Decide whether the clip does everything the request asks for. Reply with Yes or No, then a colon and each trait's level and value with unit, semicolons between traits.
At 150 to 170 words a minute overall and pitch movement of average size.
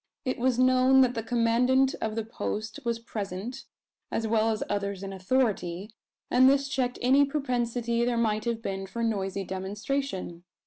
Yes: average, 165 wpm; average, 3.8 semitones